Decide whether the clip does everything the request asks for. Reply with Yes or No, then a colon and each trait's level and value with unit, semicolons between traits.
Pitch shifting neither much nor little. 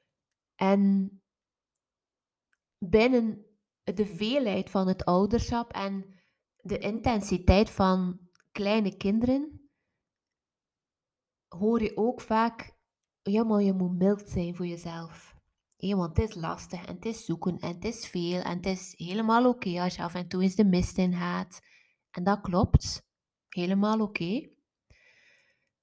Yes: average, 3.3 semitones